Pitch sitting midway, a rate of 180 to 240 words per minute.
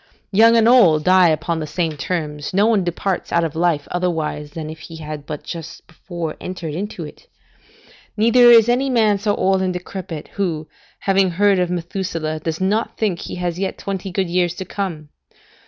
Yes: medium, 180 Hz; average, 190 wpm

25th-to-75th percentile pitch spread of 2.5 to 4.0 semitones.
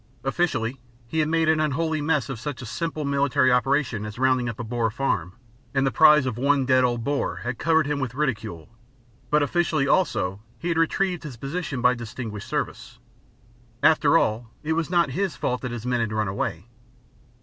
No: average, 4.7 semitones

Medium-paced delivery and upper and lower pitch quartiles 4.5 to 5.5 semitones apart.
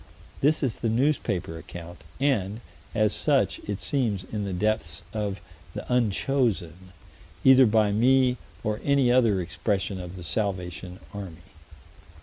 No: slow, 130 wpm; average, 5.1 semitones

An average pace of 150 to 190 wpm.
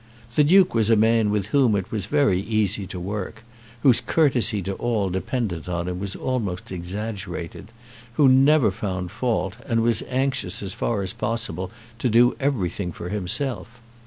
Yes: average, 165 wpm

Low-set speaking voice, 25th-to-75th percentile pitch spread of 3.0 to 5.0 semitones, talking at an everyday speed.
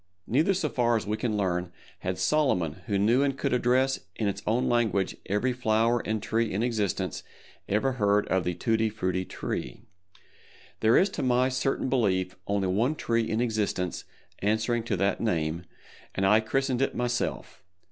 Yes: low, 110 Hz; average, 3.9 semitones; average, 170 wpm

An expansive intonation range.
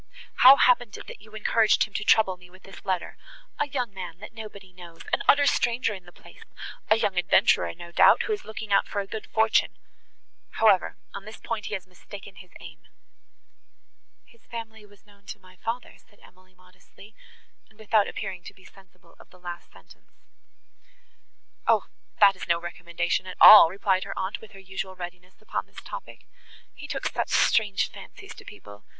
No: average, 3.1 semitones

